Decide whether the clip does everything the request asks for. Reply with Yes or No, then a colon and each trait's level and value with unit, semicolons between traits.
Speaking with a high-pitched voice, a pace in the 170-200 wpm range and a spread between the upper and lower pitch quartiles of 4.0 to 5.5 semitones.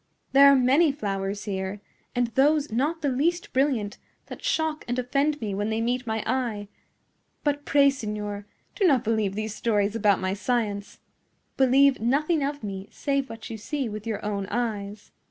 Yes: high, 235 Hz; average, 175 wpm; average, 5.1 semitones